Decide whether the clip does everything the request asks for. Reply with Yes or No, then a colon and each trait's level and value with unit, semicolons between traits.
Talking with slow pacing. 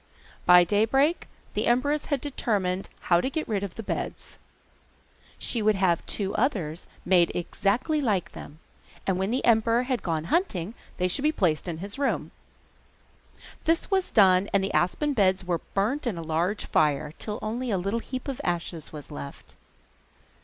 No: average, 170 wpm